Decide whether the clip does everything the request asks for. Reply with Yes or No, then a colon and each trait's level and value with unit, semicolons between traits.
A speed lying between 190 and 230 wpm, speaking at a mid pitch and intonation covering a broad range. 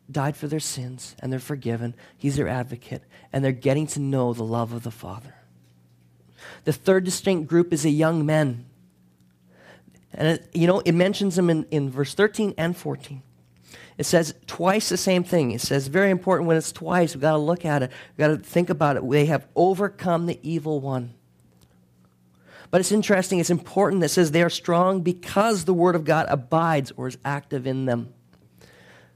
Yes: average, 195 wpm; medium, 150 Hz; wide, 6.3 semitones